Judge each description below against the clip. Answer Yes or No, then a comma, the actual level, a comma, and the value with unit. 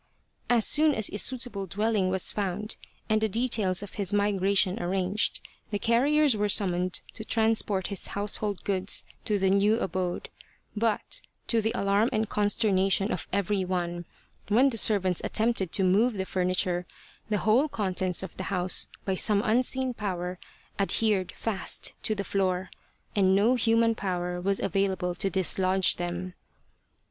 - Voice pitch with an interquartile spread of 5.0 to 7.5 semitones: No, average, 2.8 semitones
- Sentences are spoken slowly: No, average, 155 wpm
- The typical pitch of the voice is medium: No, high, 200 Hz